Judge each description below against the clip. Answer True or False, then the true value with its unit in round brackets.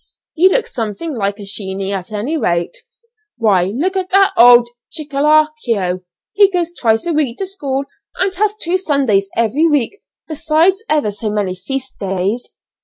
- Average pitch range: False (8.3 semitones)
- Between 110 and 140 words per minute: False (160 wpm)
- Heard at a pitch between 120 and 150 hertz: False (270 Hz)